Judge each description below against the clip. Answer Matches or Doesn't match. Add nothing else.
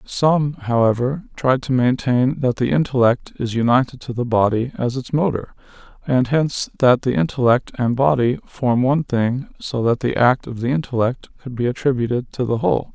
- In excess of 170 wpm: Matches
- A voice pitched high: Doesn't match